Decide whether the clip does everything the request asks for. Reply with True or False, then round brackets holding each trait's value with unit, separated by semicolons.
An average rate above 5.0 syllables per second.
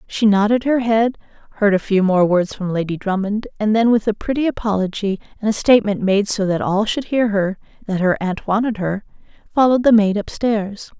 True (5.4 syllables/s)